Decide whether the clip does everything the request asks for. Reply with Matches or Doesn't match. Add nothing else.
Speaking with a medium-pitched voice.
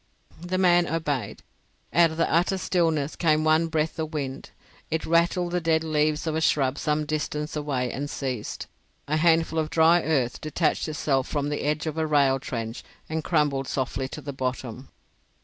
Matches